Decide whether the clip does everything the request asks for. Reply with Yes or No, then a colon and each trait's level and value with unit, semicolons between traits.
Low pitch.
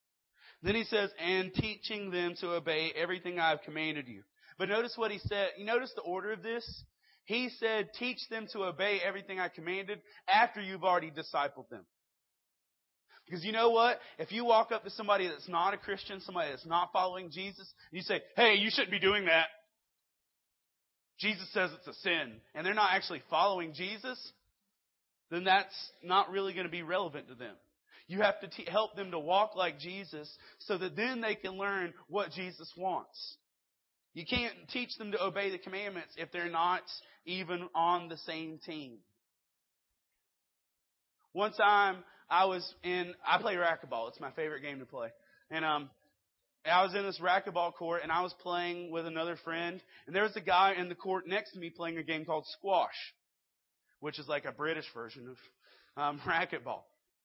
No: medium, 185 Hz